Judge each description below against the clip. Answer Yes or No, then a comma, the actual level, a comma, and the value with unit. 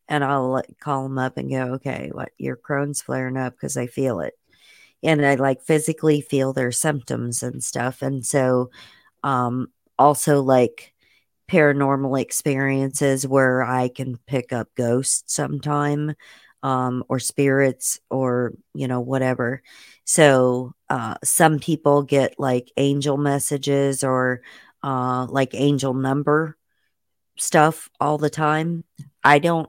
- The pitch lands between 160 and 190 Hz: No, low, 135 Hz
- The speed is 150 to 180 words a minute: No, slow, 135 wpm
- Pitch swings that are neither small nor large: No, narrow, 2.2 semitones